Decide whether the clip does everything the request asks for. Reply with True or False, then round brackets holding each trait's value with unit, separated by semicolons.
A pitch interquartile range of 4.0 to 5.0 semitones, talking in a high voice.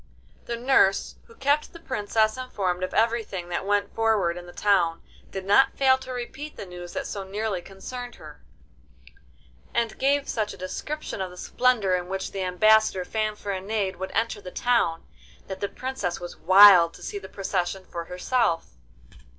True (4.3 semitones; 200 Hz)